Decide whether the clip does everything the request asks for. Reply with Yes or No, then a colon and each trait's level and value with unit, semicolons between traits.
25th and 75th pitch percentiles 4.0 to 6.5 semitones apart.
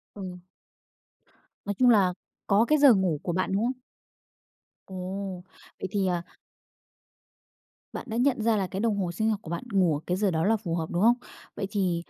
No: average, 3.4 semitones